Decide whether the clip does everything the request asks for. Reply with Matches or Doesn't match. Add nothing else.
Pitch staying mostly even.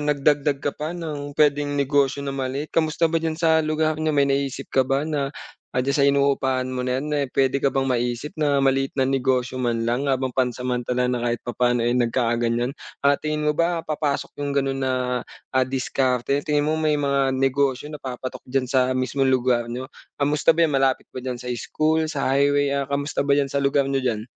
Matches